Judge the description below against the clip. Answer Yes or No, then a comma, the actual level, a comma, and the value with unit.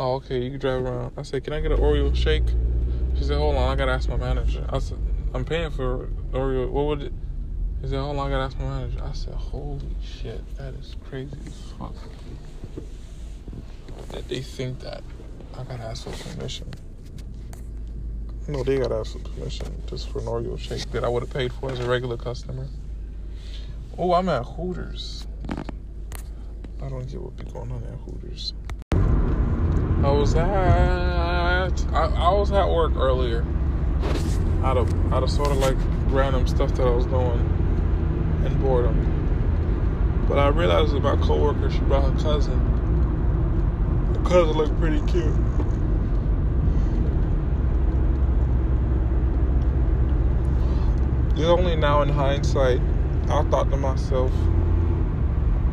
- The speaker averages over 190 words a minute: No, average, 150 wpm